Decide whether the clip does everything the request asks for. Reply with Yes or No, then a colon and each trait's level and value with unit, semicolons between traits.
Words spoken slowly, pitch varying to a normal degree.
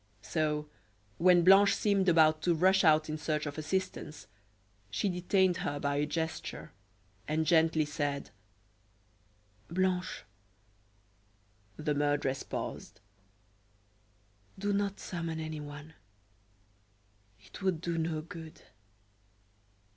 Yes: slow, 100 wpm; average, 3.1 semitones